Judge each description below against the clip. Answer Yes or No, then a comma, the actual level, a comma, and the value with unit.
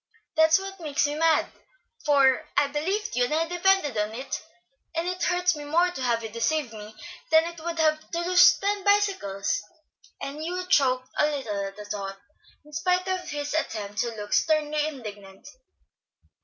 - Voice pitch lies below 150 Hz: No, very high, 300 Hz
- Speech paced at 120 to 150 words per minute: No, average, 170 wpm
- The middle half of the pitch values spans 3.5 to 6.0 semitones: No, wide, 6.6 semitones